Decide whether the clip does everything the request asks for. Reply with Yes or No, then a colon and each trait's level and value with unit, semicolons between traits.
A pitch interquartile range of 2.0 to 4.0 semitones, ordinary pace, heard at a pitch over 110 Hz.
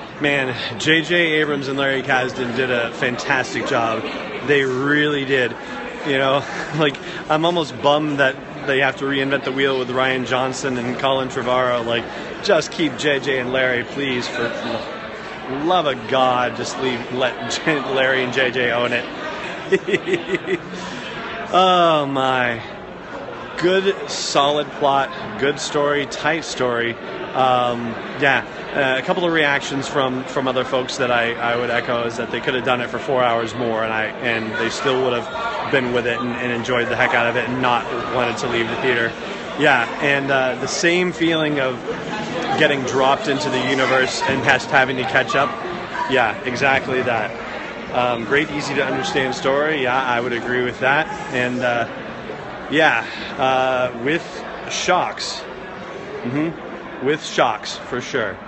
Yes: average, 2.8 semitones; average, 160 wpm; low, 130 Hz